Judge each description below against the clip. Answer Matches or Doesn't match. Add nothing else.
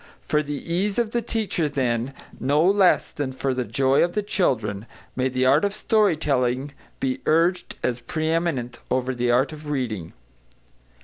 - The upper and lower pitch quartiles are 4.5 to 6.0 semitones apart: Matches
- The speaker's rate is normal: Matches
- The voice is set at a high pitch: Doesn't match